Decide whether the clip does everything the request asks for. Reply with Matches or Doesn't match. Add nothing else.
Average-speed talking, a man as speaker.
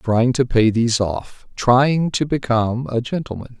Matches